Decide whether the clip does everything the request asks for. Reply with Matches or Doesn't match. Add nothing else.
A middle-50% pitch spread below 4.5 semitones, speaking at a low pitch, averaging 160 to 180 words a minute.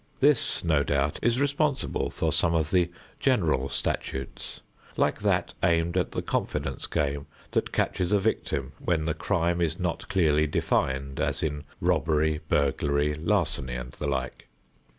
Doesn't match